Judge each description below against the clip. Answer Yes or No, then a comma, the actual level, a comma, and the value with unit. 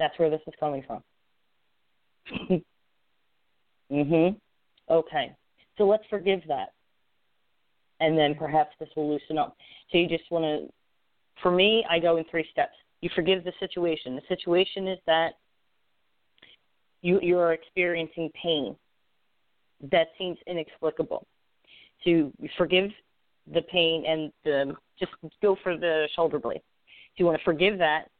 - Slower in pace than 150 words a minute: Yes, average, 140 wpm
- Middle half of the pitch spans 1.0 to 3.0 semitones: Yes, narrow, 2.6 semitones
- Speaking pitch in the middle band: Yes, medium, 165 Hz